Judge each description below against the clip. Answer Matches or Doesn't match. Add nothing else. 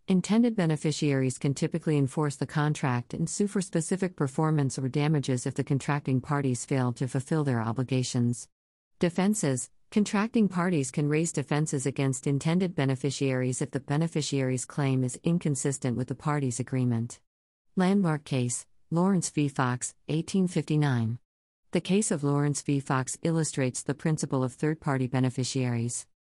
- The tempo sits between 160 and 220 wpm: Doesn't match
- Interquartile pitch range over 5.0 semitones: Doesn't match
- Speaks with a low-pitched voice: Doesn't match